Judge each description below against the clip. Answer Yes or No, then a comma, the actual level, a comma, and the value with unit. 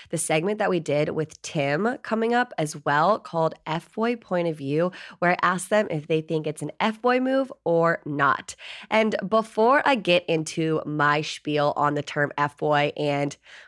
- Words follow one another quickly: No, average, 195 wpm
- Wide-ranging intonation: Yes, wide, 6.3 semitones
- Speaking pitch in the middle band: Yes, medium, 165 Hz